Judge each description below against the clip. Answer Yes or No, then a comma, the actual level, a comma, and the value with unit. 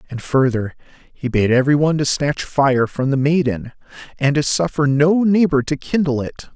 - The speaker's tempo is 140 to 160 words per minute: No, average, 185 wpm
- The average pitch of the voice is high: No, medium, 140 Hz